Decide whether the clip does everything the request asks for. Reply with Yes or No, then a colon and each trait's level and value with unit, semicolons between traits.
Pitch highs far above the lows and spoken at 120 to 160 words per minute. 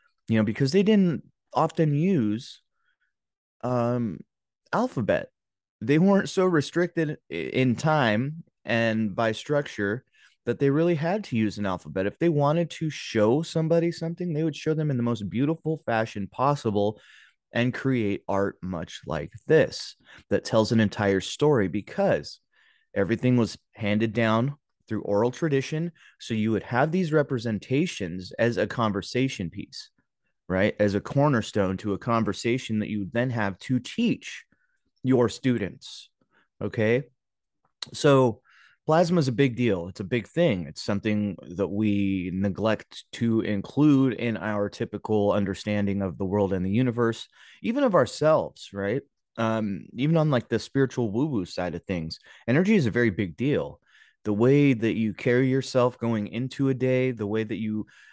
Yes: wide, 5.7 semitones; average, 155 wpm